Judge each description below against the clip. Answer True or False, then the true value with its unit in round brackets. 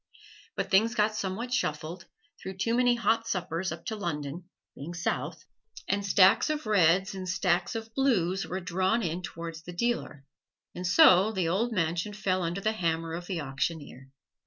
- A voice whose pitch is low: False (185 Hz)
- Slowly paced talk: False (170 wpm)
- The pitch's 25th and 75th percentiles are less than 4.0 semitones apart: False (4.3 semitones)